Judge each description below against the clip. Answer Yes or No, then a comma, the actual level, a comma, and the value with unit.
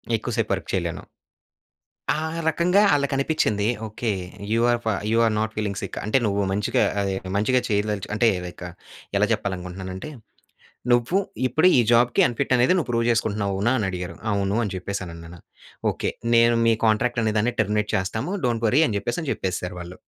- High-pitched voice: No, low, 110 Hz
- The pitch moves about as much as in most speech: Yes, average, 3.5 semitones